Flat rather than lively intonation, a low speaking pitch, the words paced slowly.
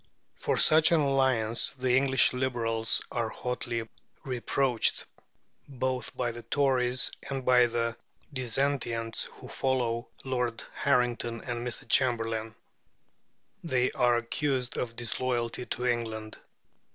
Yes: narrow, 2.0 semitones; low, 125 Hz; slow, 115 wpm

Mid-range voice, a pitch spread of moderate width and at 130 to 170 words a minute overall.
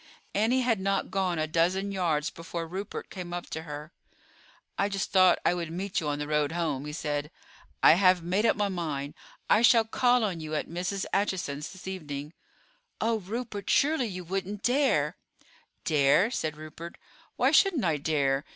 No: medium, 180 Hz; average, 4.5 semitones; average, 180 wpm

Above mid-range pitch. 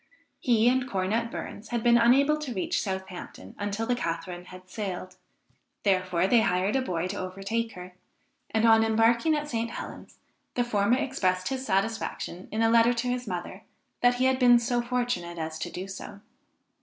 Yes: high, 225 Hz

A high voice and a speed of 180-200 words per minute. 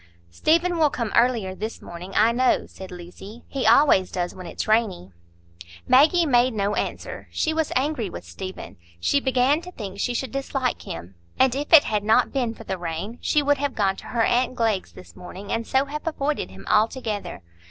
Yes: high, 230 Hz; average, 195 wpm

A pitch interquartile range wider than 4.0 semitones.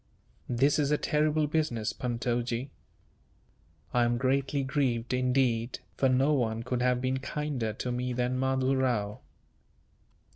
No: narrow, 2.4 semitones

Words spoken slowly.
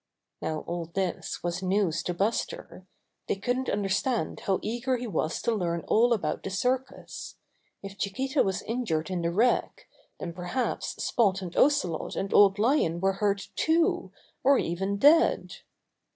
No: average, 150 wpm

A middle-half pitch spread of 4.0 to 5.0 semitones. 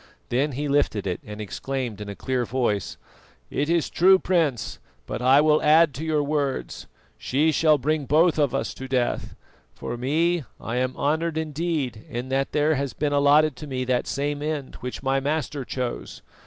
No: average, 3.2 semitones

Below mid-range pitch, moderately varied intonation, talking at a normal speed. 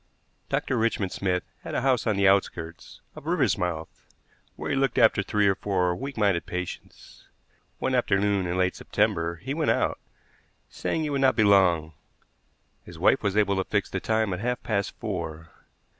Yes: low, 100 Hz; average, 3.6 semitones; average, 175 wpm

